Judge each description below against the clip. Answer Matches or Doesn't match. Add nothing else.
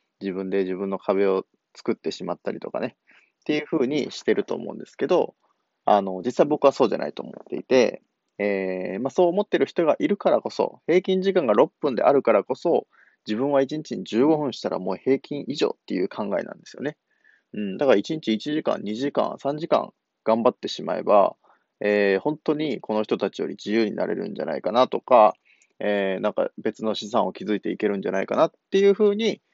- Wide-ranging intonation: Matches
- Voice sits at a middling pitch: Doesn't match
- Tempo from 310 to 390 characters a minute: Matches